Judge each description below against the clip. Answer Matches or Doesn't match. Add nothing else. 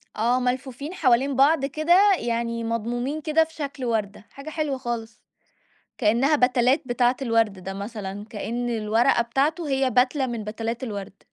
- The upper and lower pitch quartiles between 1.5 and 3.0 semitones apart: Doesn't match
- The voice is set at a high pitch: Matches